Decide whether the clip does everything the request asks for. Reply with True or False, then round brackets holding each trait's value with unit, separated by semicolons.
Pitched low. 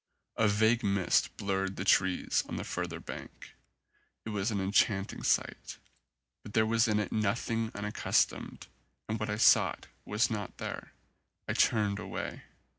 True (105 Hz)